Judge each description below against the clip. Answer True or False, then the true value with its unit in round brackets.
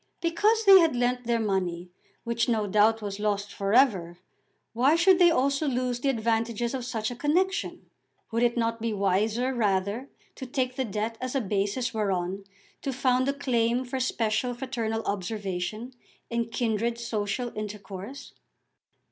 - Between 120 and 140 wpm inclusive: False (155 wpm)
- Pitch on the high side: True (235 Hz)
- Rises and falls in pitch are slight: False (3.6 semitones)